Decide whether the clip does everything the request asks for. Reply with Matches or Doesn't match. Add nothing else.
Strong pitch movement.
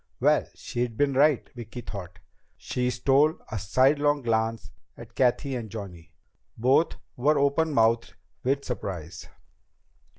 Doesn't match